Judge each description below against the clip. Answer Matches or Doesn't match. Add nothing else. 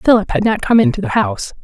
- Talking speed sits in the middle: Doesn't match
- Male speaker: Doesn't match